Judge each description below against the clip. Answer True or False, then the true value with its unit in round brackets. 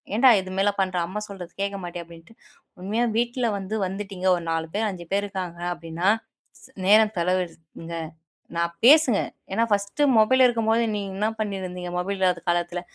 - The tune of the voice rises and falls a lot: False (3.3 semitones)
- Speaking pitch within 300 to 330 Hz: False (195 Hz)